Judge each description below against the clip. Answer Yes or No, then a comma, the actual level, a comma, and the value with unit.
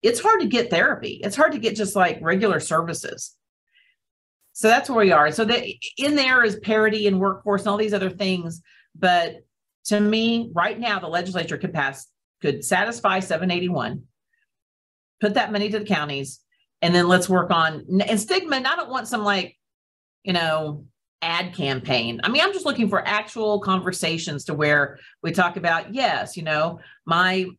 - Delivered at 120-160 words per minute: No, average, 185 wpm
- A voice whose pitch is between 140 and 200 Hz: Yes, high, 190 Hz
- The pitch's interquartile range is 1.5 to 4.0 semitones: No, average, 4.7 semitones